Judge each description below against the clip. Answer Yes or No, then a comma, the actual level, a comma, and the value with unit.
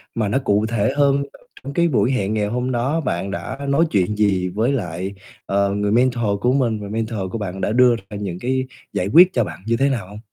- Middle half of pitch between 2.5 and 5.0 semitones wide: Yes, average, 4.2 semitones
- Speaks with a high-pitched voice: No, low, 110 Hz